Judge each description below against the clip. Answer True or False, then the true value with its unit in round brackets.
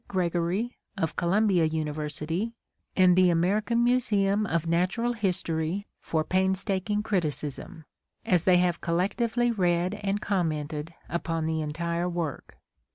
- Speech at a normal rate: False (115 wpm)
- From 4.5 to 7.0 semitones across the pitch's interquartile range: False (3.6 semitones)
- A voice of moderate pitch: True (180 Hz)